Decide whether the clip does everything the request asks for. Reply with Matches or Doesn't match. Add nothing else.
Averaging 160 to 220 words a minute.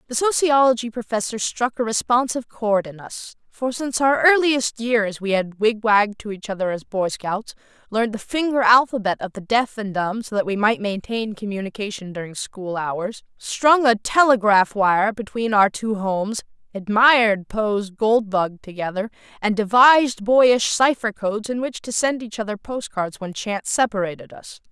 Matches